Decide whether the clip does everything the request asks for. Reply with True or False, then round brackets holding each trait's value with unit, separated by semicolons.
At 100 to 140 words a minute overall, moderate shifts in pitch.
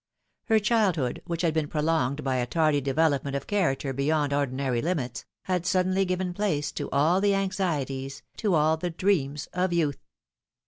False (170 wpm; 4.8 semitones)